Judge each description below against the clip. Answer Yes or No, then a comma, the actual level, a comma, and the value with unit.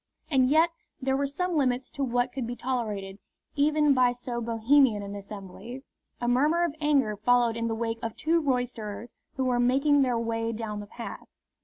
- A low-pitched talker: No, high, 245 Hz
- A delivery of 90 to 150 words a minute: No, average, 185 wpm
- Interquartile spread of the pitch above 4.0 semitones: No, average, 3.4 semitones